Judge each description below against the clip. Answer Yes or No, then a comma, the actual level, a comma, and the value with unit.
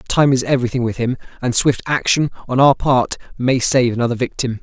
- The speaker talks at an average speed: Yes, average, 195 wpm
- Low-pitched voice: Yes, low, 125 Hz